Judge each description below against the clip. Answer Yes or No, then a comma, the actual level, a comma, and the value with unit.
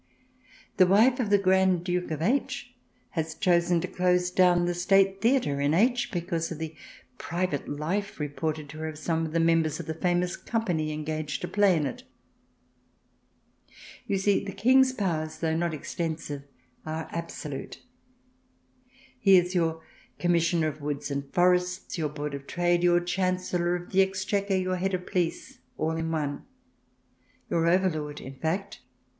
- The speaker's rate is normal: Yes, average, 160 wpm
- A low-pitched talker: No, medium, 175 Hz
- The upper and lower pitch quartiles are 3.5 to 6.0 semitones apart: No, average, 3.1 semitones